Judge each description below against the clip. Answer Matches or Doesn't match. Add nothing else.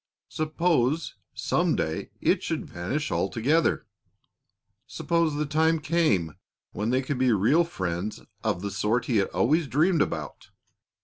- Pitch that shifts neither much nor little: Doesn't match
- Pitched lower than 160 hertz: Matches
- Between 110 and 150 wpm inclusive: Matches